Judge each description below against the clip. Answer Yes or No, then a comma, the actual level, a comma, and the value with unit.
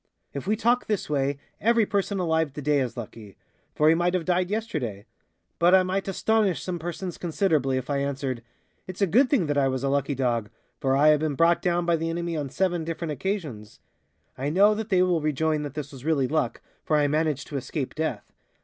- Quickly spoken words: Yes, fast, 215 wpm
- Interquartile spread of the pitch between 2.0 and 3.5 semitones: No, average, 4.8 semitones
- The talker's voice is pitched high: No, medium, 160 Hz